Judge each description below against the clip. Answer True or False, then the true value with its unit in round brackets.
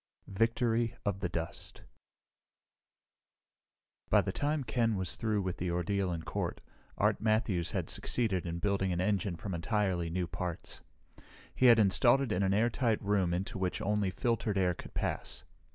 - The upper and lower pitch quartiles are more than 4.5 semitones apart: False (3.9 semitones)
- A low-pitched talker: True (100 Hz)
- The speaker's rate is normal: True (160 wpm)